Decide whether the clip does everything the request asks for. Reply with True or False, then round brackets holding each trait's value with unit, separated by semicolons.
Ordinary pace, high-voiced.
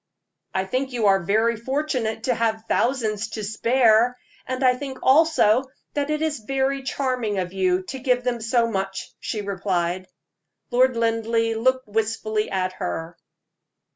True (150 wpm; 230 Hz)